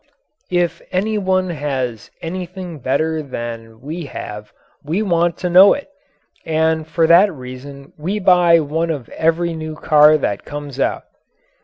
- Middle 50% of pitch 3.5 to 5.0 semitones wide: Yes, average, 3.8 semitones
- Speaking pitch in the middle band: Yes, medium, 160 Hz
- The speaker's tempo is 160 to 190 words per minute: No, average, 145 wpm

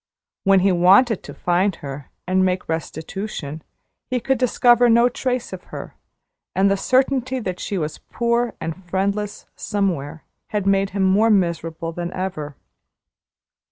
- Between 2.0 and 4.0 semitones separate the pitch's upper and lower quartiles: No, average, 4.7 semitones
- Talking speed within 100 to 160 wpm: Yes, average, 145 wpm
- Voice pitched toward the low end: No, high, 195 Hz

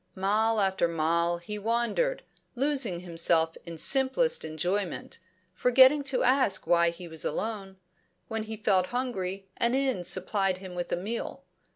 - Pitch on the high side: Yes, high, 195 Hz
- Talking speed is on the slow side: No, average, 145 wpm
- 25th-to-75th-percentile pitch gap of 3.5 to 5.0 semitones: No, wide, 5.6 semitones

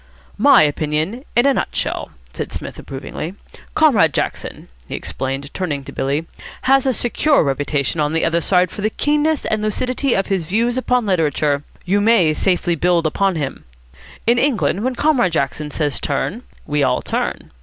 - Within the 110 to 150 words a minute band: No, average, 165 wpm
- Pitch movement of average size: No, wide, 8.1 semitones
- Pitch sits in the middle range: Yes, medium, 180 Hz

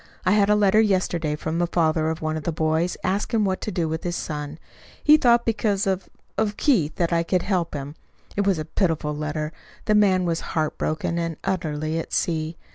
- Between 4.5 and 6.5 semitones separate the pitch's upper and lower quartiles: No, average, 3.9 semitones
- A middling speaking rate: No, fast, 210 wpm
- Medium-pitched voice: Yes, medium, 170 Hz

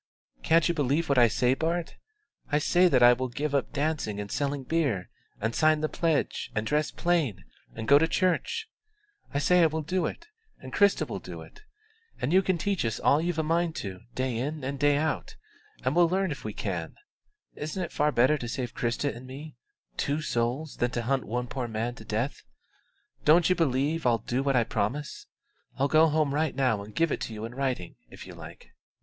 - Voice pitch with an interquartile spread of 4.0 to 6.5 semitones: Yes, average, 4.8 semitones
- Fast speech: Yes, fast, 215 wpm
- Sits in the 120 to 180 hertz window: Yes, medium, 140 Hz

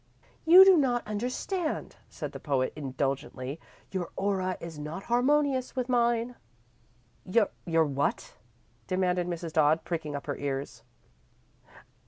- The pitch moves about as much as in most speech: No, wide, 8.3 semitones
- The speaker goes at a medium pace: No, slow, 120 wpm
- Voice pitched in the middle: Yes, medium, 180 Hz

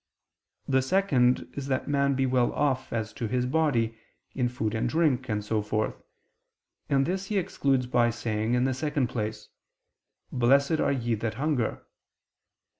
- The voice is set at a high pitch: No, low, 125 Hz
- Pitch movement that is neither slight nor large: Yes, average, 3.3 semitones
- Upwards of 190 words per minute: No, average, 155 wpm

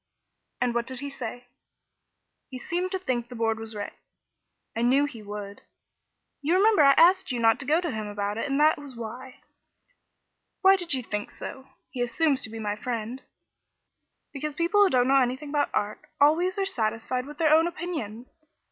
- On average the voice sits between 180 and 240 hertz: No, very high, 260 Hz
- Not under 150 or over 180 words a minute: No, average, 190 wpm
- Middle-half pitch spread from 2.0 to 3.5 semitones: No, wide, 5.4 semitones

